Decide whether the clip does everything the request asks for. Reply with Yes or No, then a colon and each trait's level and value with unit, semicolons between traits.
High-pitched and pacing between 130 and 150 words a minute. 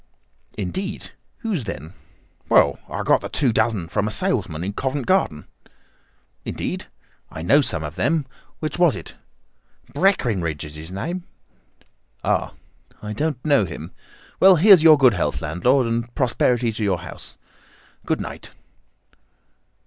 No: low, 120 Hz; average, 140 wpm